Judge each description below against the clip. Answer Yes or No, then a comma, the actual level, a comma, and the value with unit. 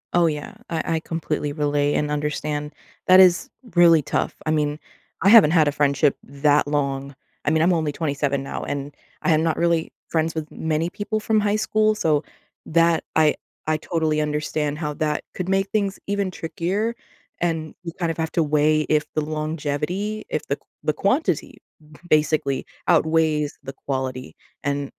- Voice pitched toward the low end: No, medium, 155 Hz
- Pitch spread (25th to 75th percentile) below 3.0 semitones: Yes, narrow, 2.5 semitones